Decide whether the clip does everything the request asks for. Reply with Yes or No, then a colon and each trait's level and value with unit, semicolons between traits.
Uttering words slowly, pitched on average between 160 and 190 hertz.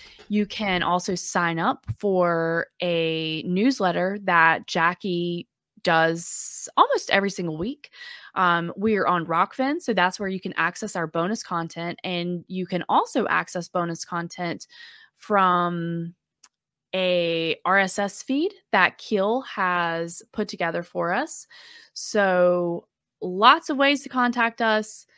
Yes: slow, 130 wpm; medium, 185 Hz